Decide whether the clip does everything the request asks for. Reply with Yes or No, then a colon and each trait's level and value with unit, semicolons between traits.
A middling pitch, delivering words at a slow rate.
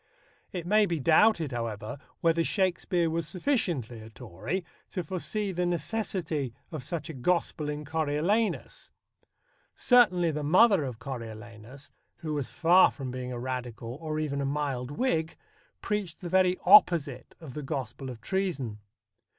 No: medium, 155 Hz; average, 145 wpm